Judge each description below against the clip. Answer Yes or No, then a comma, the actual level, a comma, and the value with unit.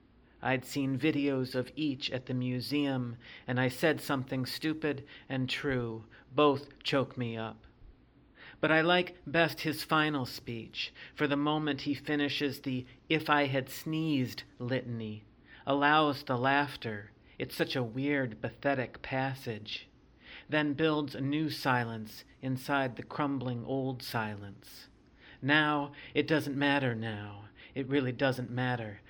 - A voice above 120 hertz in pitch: Yes, low, 135 Hz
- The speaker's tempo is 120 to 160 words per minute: Yes, slow, 135 wpm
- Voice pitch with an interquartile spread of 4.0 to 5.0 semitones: No, average, 2.8 semitones